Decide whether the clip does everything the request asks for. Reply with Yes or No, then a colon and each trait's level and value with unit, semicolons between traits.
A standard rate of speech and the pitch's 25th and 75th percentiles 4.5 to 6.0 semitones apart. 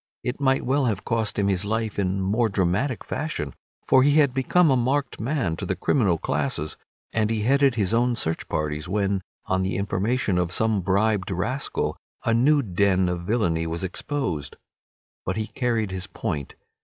Yes: average, 180 wpm; average, 5.1 semitones